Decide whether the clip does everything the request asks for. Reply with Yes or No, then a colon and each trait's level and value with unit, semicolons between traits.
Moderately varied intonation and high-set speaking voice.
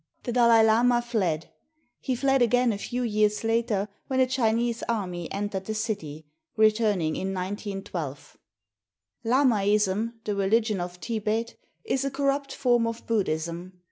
Yes: average, 3.6 semitones; high, 220 Hz